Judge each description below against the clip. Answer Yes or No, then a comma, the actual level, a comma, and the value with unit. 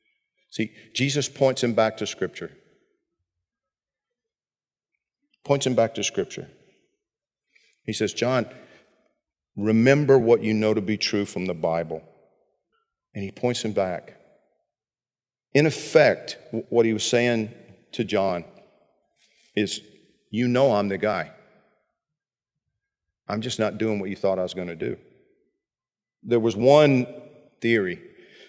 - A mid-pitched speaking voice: No, low, 115 Hz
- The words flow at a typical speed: No, slow, 125 wpm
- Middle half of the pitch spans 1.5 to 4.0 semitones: No, average, 4.8 semitones